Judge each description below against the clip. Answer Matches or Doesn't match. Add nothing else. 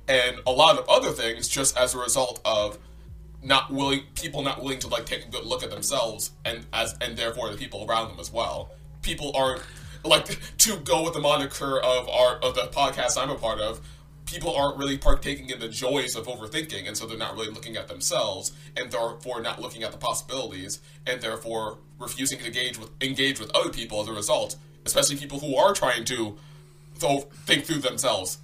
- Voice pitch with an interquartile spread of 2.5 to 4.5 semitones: Matches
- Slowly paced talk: Doesn't match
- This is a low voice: Matches